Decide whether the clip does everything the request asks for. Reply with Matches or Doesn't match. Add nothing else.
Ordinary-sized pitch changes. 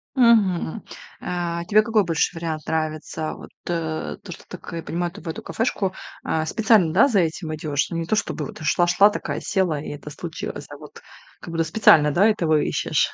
Matches